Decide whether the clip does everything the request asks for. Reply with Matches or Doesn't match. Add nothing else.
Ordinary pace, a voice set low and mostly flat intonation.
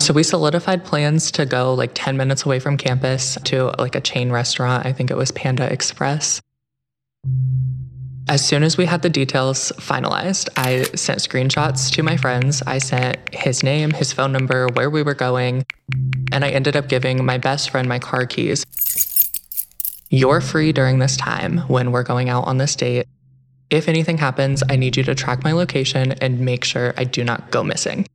Matches